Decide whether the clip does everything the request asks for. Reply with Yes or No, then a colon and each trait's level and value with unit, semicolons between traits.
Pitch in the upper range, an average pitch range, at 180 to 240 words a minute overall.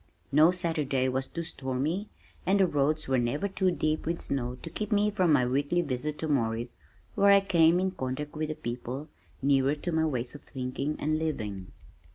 No: medium, 150 Hz; average, 4.6 semitones; average, 190 wpm